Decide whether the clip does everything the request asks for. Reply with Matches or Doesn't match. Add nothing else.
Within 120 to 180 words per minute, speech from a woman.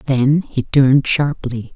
Matches